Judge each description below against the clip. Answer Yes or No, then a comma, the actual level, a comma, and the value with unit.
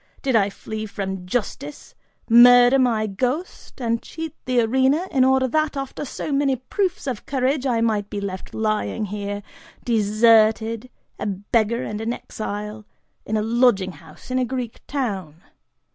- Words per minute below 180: Yes, average, 155 wpm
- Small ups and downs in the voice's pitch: No, average, 3.8 semitones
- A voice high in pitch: Yes, high, 230 Hz